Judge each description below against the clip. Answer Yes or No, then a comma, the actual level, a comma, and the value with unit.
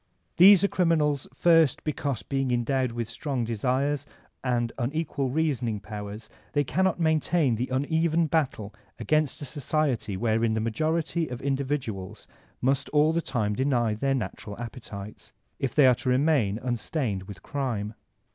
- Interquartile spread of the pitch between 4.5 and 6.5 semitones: Yes, average, 4.8 semitones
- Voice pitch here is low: Yes, low, 130 Hz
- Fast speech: No, average, 145 wpm